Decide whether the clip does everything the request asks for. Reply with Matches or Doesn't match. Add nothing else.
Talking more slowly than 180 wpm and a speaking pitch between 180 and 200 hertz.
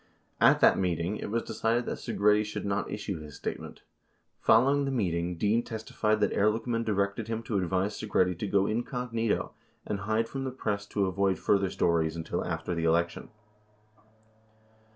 Doesn't match